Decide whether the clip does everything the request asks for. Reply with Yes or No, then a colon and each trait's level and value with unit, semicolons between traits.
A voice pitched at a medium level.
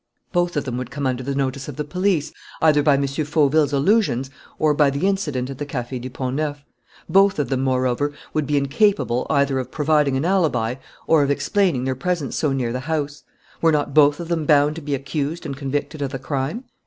Yes: medium, 145 Hz